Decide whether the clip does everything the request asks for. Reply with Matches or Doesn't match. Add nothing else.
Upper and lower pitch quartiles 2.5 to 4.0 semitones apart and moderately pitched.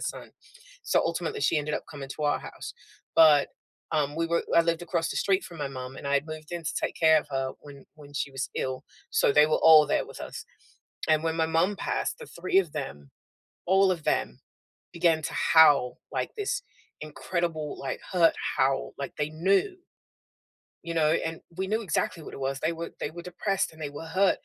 Matches